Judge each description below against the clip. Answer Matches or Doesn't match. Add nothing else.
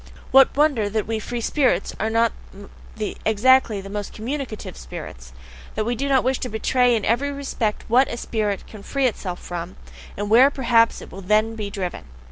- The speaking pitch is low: Doesn't match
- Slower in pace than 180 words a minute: Doesn't match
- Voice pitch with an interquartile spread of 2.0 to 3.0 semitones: Doesn't match